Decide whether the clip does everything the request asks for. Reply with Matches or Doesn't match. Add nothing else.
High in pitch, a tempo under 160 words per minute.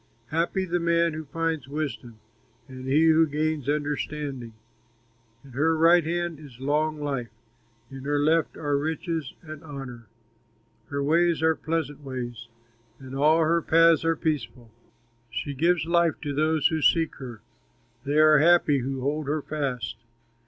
Doesn't match